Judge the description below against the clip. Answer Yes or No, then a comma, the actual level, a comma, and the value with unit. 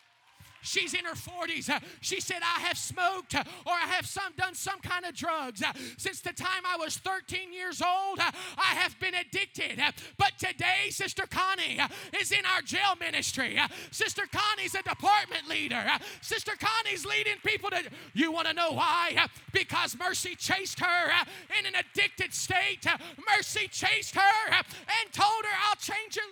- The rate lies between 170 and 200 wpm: No, average, 160 wpm